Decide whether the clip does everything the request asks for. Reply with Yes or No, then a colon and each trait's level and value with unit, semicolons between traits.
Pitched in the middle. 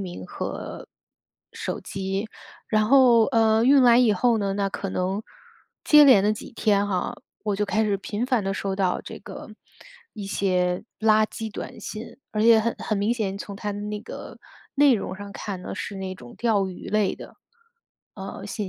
No: high, 210 Hz